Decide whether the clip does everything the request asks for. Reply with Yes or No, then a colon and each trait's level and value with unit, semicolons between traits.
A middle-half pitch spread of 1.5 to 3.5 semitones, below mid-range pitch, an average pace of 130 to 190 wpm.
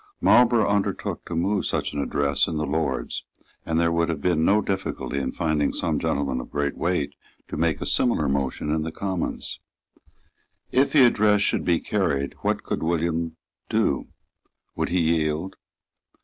No: average, 4.1 semitones; very low, 85 Hz; average, 165 wpm